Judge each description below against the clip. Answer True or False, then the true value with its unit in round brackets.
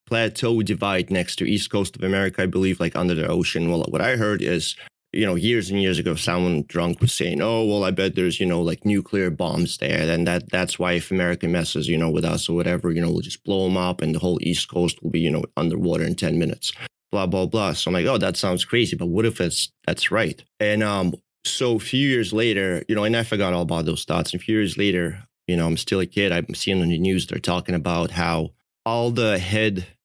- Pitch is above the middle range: False (90 Hz)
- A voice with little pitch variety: False (3.3 semitones)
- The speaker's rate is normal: False (255 wpm)